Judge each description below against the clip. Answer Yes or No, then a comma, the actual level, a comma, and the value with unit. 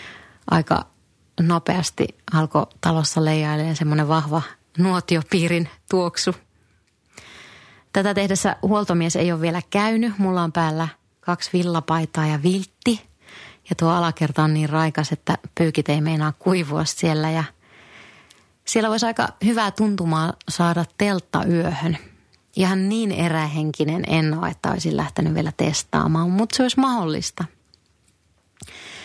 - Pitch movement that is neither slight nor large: Yes, average, 3.1 semitones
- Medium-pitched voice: Yes, medium, 165 Hz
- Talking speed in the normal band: Yes, average, 120 wpm